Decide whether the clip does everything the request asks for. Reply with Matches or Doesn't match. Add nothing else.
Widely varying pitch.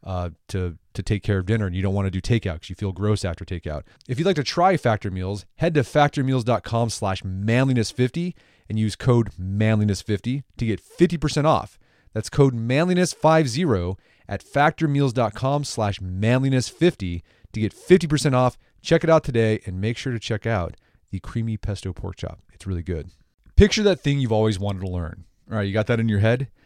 Matches